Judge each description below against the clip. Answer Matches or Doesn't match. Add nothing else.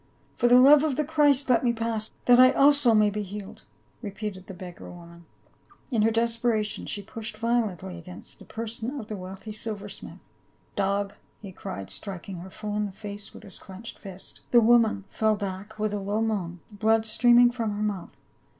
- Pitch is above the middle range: Matches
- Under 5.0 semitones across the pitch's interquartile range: Matches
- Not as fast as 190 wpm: Doesn't match